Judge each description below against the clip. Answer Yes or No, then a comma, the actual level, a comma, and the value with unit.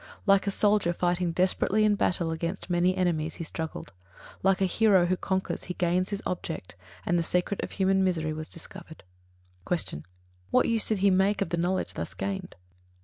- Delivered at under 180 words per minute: No, average, 190 wpm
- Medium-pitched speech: Yes, medium, 180 Hz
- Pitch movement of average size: No, narrow, 2.2 semitones